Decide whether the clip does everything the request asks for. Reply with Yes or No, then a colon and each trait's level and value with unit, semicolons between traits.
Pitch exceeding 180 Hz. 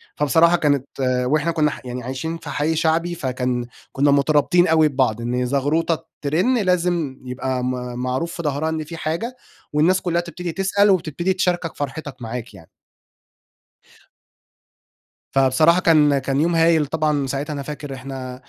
No: medium, 150 Hz